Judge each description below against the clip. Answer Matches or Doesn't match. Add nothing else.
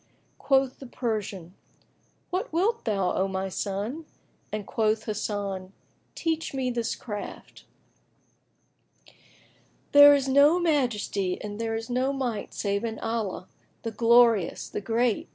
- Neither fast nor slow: Doesn't match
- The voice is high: Matches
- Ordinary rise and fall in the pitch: Matches